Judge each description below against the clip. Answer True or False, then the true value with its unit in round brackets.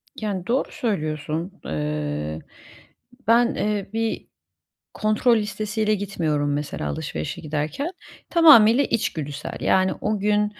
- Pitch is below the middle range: False (200 Hz)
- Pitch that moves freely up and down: True (6.6 semitones)